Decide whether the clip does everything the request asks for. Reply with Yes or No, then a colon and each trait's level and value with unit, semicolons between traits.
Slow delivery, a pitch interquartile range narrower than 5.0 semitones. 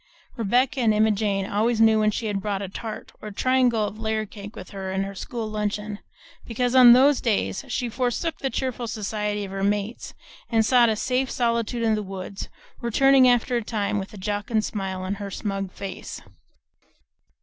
No: average, 185 wpm; average, 2.9 semitones